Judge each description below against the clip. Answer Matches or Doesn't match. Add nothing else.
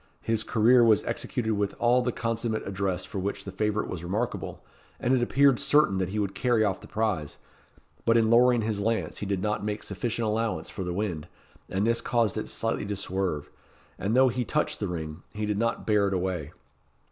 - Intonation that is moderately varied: Matches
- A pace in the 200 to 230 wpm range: Matches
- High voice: Doesn't match